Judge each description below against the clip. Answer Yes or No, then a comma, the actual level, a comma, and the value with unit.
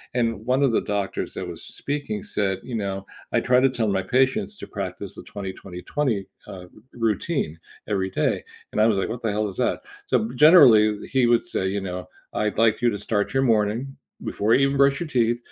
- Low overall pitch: Yes, low, 115 Hz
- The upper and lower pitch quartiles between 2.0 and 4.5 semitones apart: No, average, 4.9 semitones